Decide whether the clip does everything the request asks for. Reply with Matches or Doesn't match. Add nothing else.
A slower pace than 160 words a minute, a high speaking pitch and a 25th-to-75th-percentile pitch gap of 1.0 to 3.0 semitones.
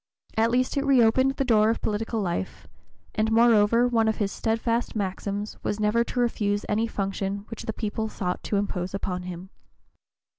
Doesn't match